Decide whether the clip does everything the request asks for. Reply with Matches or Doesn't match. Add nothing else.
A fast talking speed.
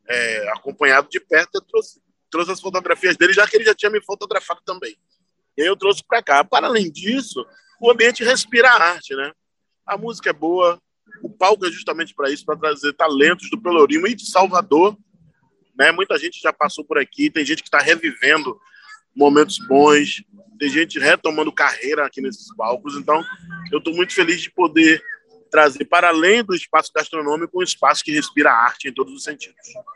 Matches